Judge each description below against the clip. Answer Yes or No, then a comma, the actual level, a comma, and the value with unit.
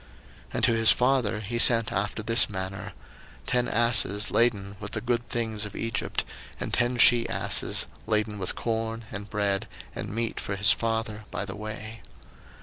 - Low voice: Yes, low, 110 Hz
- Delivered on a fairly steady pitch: Yes, narrow, 2.1 semitones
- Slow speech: No, average, 170 wpm